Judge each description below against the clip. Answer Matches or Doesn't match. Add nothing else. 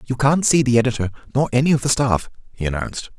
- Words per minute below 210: Doesn't match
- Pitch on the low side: Matches